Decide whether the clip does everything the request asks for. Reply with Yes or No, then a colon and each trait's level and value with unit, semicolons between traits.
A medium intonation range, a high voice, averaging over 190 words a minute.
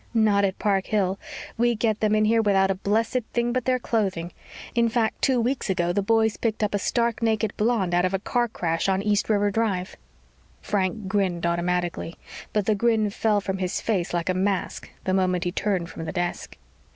Yes: average, 3.2 semitones; high, 205 Hz; fast, 205 wpm